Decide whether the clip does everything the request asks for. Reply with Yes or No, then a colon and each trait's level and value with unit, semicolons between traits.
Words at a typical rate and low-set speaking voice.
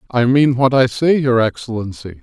Yes: average, 190 wpm; low, 125 Hz